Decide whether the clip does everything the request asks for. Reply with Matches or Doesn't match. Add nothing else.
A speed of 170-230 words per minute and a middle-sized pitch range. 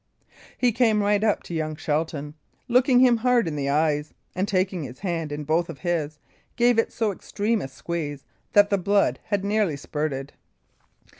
Doesn't match